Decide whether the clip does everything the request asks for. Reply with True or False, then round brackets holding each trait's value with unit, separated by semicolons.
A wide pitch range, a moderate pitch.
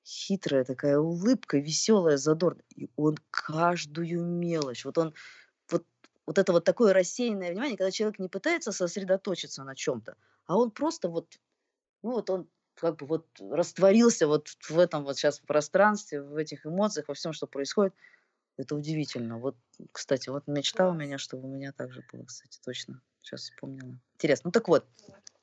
False (4.9 semitones; 165 Hz)